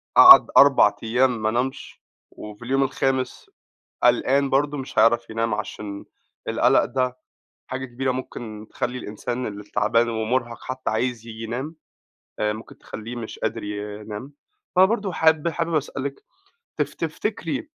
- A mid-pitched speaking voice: No, low, 125 Hz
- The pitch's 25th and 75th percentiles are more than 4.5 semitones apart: No, average, 3.5 semitones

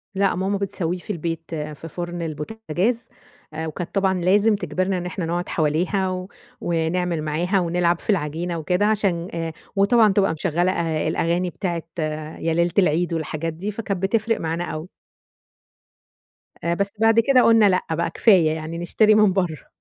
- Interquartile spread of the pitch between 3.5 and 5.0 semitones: No, average, 3.1 semitones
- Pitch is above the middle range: No, medium, 175 Hz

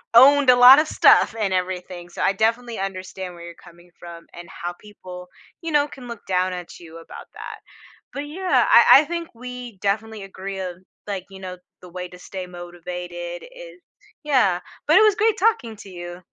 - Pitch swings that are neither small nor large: No, wide, 5.8 semitones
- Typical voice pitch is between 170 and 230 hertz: Yes, high, 190 Hz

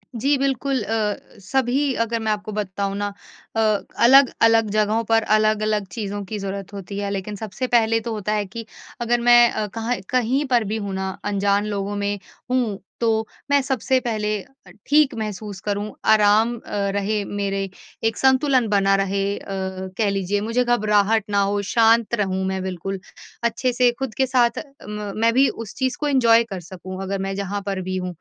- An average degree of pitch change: Yes, average, 3.1 semitones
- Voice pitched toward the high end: Yes, high, 215 Hz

